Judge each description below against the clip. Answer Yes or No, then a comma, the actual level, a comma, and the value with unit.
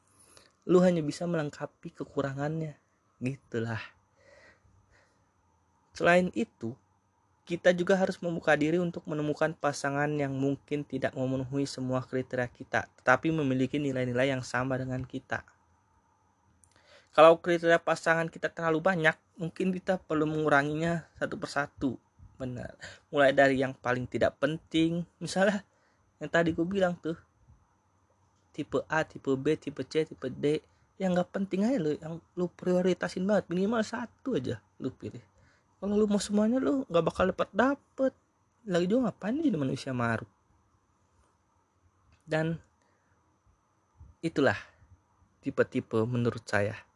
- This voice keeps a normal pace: Yes, average, 125 wpm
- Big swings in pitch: Yes, wide, 7.5 semitones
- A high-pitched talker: No, medium, 140 Hz